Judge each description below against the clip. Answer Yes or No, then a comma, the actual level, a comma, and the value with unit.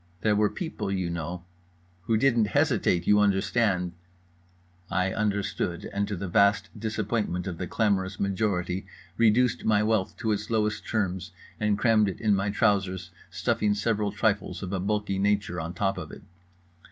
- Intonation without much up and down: Yes, narrow, 2.3 semitones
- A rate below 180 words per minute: Yes, average, 160 wpm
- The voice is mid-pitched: No, low, 100 Hz